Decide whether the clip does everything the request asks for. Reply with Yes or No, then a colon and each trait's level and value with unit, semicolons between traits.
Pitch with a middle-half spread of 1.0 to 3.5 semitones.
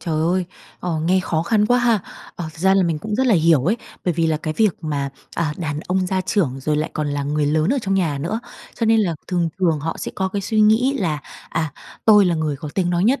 No: average, 4.7 semitones